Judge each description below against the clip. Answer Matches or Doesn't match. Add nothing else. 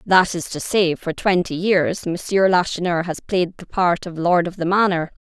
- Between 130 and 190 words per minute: Doesn't match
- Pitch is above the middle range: Doesn't match